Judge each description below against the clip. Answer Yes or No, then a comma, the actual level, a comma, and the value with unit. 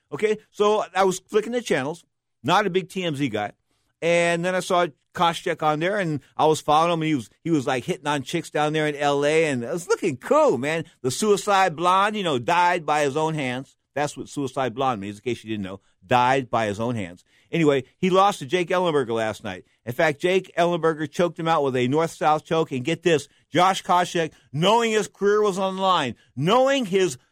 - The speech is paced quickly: Yes, fast, 220 wpm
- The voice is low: No, medium, 160 Hz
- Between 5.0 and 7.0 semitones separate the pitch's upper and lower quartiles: Yes, wide, 5.6 semitones